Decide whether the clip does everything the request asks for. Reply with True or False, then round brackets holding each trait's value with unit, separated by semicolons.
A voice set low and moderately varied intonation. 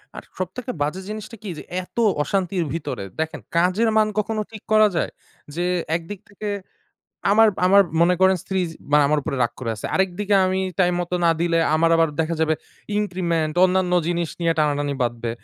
False (175 Hz; 3.6 semitones)